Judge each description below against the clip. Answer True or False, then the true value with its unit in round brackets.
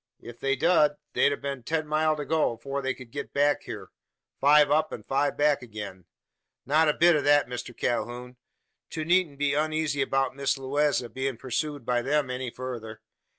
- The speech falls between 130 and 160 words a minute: False (185 wpm)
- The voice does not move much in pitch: False (3.3 semitones)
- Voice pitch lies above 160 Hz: False (140 Hz)